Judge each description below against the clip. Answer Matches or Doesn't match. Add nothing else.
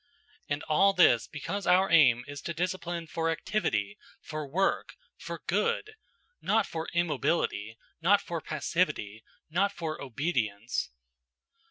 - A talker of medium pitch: Matches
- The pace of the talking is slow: Matches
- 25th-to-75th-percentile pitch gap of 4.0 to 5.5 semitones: Matches